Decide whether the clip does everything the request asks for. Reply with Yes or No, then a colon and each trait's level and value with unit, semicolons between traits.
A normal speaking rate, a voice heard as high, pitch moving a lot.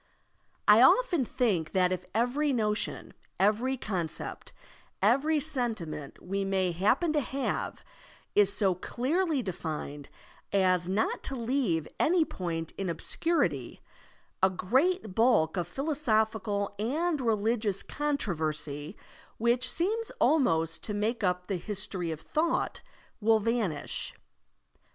No: slow, 115 wpm; high, 215 Hz; wide, 6.6 semitones